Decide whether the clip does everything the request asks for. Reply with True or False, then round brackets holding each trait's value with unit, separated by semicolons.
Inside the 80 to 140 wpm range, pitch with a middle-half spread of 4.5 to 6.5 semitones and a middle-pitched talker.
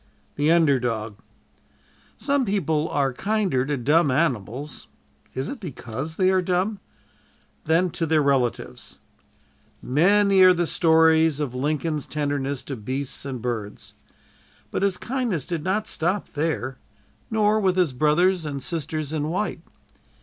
True (135 wpm; 5.2 semitones; 155 Hz)